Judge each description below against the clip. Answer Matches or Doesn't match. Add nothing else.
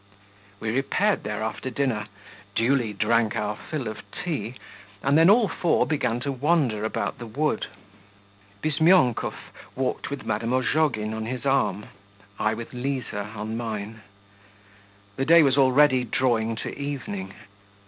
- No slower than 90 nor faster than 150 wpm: Matches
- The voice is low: Matches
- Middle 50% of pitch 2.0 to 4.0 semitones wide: Doesn't match